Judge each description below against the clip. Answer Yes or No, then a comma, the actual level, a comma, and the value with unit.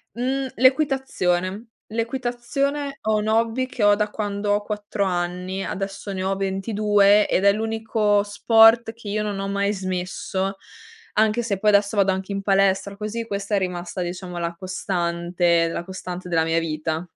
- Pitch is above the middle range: Yes, high, 200 Hz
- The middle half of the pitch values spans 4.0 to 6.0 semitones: No, average, 2.9 semitones